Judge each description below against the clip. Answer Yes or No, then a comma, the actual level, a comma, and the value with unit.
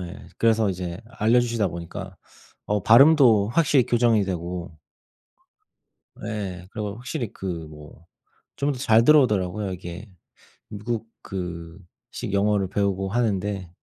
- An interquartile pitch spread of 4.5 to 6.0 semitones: No, average, 4.1 semitones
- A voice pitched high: No, low, 100 Hz